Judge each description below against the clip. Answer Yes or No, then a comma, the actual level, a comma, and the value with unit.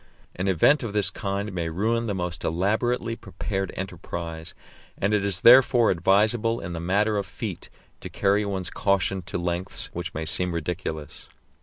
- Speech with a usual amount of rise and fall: Yes, average, 3.4 semitones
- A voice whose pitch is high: No, very low, 95 Hz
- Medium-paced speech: Yes, average, 165 wpm